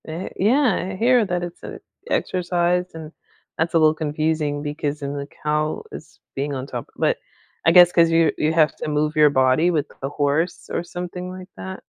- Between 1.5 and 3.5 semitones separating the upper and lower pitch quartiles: Yes, average, 3.2 semitones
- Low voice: No, medium, 160 Hz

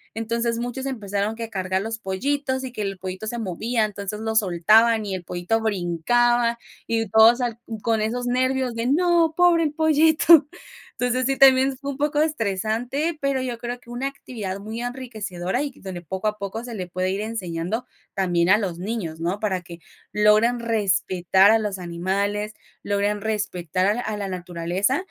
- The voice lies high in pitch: Yes, high, 220 Hz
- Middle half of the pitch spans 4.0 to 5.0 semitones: Yes, average, 4.4 semitones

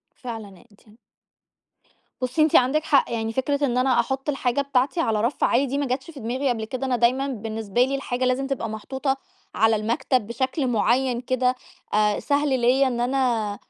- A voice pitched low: No, very high, 255 Hz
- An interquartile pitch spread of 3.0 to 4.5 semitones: No, narrow, 2.6 semitones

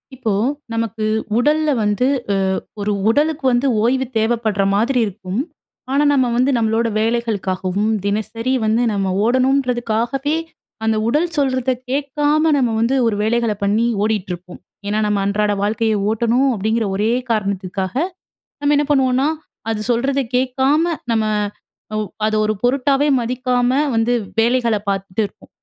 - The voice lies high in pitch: Yes, high, 230 Hz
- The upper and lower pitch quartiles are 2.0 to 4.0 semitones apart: Yes, average, 3.6 semitones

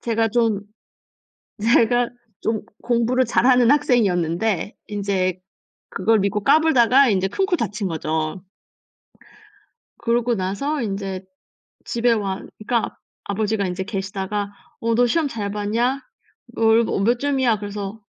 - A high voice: Yes, high, 220 Hz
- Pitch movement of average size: Yes, average, 3.4 semitones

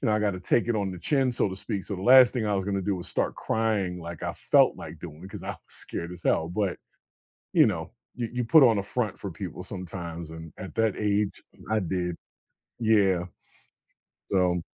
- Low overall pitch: Yes, very low, 95 Hz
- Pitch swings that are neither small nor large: Yes, average, 3.6 semitones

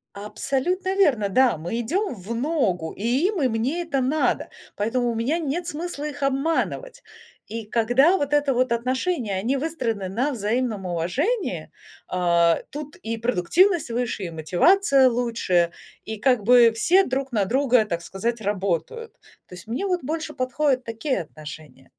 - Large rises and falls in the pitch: Yes, wide, 6.3 semitones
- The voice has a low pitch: No, very high, 250 Hz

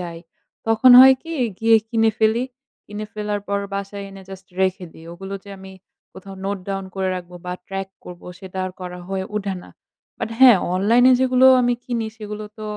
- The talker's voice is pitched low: No, high, 200 Hz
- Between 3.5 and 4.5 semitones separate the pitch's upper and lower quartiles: No, average, 2.8 semitones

